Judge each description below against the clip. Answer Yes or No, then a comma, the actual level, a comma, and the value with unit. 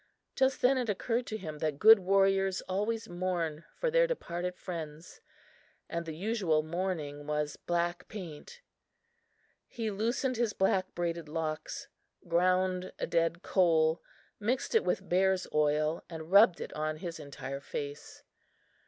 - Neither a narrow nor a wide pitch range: Yes, average, 4.1 semitones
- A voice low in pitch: No, medium, 180 Hz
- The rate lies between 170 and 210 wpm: No, average, 140 wpm